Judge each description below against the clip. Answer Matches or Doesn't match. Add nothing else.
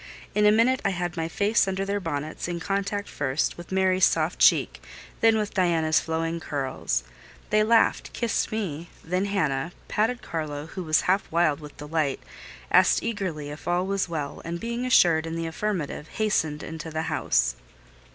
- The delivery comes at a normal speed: Matches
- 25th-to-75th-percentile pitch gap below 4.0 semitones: Doesn't match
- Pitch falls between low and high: Matches